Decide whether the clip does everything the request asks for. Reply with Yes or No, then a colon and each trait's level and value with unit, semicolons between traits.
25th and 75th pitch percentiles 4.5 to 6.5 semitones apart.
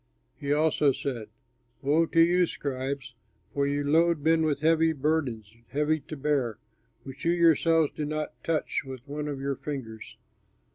No: average, 2.7 semitones